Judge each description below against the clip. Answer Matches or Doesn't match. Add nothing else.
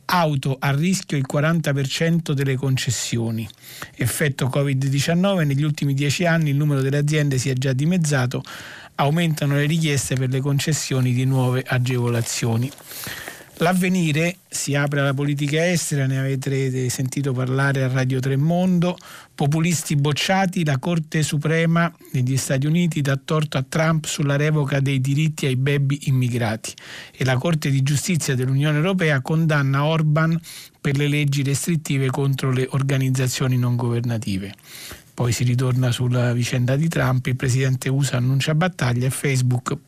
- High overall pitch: Doesn't match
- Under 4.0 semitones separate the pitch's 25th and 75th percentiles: Matches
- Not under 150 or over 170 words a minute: Doesn't match